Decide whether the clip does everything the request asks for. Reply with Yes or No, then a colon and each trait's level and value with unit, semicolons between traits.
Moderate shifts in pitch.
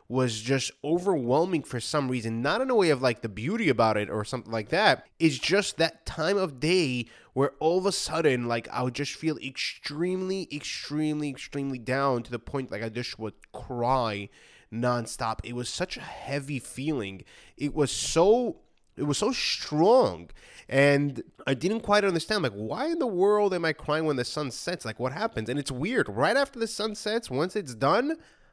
No: wide, 6.1 semitones